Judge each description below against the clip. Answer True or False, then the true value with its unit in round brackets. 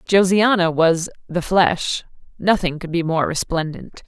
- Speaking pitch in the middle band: True (175 Hz)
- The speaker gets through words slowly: True (130 wpm)